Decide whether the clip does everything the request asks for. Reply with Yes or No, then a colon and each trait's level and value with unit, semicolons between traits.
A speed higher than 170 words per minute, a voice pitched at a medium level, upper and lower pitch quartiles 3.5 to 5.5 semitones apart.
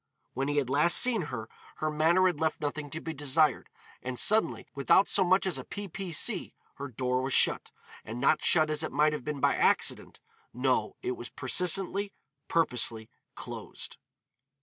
Yes: average, 180 wpm; medium, 150 Hz; average, 4.8 semitones